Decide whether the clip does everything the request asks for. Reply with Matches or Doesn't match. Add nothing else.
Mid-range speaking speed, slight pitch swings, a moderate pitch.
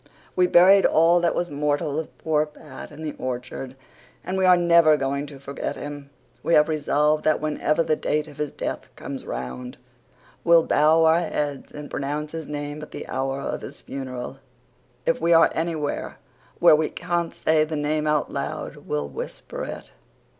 Matches